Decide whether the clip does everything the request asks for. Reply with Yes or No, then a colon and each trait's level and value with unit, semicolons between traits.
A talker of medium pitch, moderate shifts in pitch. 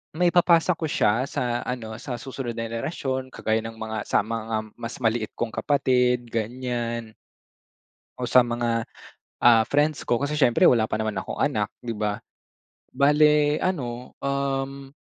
No: low, 120 Hz; average, 3.5 semitones